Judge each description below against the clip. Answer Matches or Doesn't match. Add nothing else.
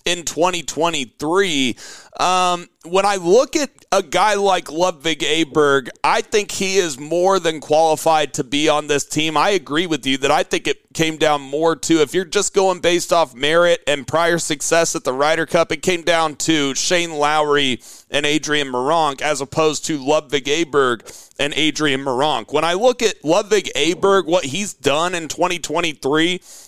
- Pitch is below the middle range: Doesn't match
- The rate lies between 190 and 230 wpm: Doesn't match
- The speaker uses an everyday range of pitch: Matches